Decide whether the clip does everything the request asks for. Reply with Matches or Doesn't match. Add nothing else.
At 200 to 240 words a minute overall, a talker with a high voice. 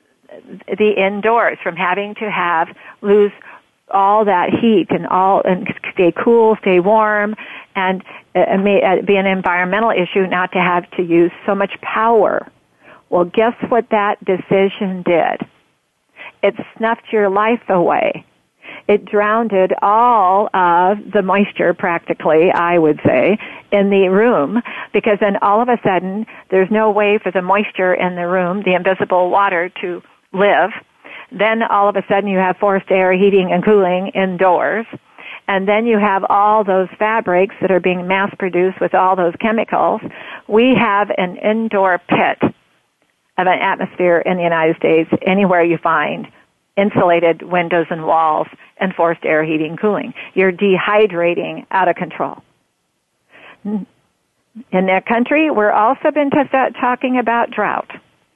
Doesn't match